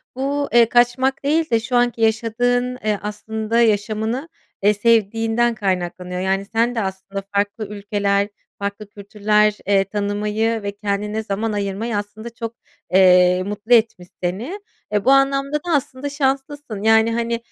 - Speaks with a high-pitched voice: Yes, high, 220 Hz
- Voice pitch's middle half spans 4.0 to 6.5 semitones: No, average, 2.9 semitones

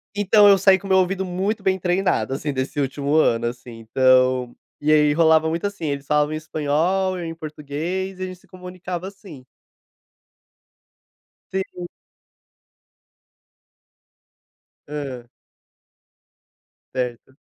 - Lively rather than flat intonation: No, average, 4.9 semitones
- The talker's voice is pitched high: No, medium, 160 Hz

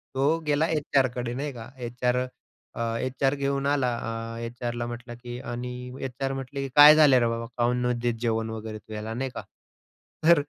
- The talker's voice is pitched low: Yes, low, 125 Hz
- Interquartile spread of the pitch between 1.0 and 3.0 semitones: Yes, narrow, 2.5 semitones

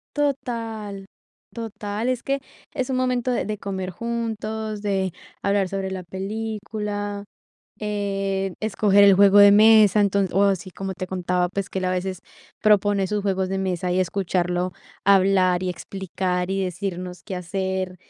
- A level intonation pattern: Yes, narrow, 2.2 semitones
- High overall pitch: Yes, high, 195 Hz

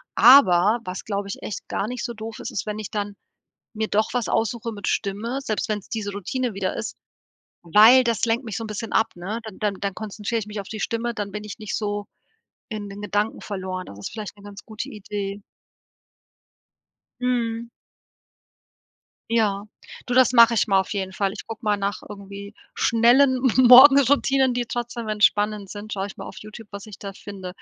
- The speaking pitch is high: Yes, high, 215 Hz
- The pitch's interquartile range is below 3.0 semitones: Yes, narrow, 2.5 semitones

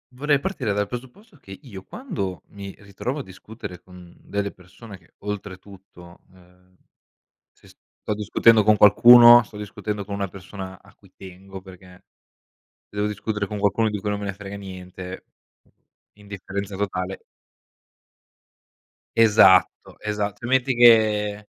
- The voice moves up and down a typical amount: No, narrow, 2.3 semitones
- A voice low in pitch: Yes, low, 100 Hz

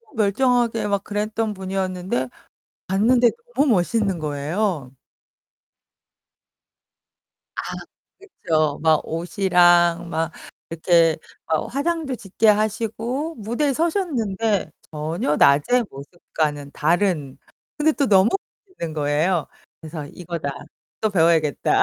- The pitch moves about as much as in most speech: No, wide, 5.9 semitones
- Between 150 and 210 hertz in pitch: Yes, high, 190 Hz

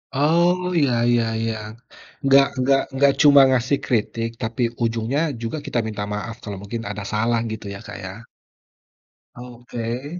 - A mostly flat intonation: No, average, 3.3 semitones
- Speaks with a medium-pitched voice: No, low, 120 Hz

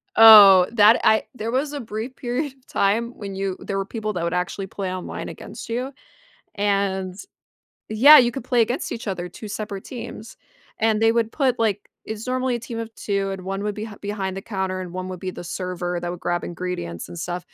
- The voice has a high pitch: Yes, high, 205 Hz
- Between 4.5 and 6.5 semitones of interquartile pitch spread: No, average, 3.6 semitones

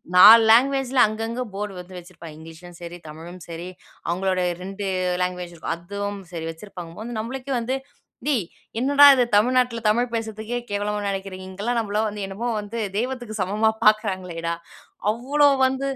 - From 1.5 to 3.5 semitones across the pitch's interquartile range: No, average, 4.6 semitones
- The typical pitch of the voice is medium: No, high, 205 Hz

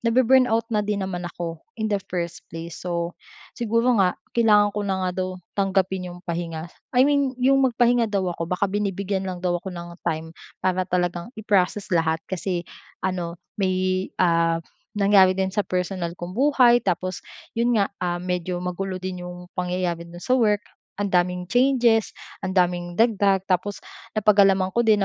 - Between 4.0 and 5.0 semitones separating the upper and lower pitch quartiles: No, average, 2.9 semitones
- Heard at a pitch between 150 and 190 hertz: Yes, medium, 185 Hz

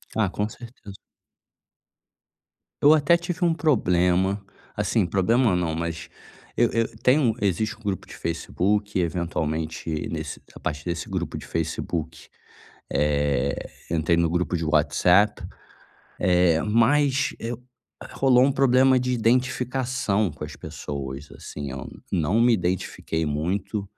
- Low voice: Yes, very low, 95 Hz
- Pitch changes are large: Yes, wide, 6.6 semitones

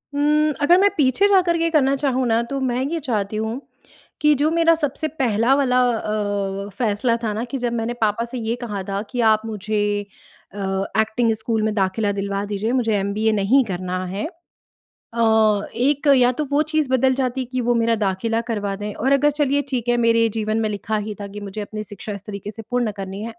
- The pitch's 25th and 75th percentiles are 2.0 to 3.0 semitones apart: No, average, 4.0 semitones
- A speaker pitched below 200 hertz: No, high, 230 Hz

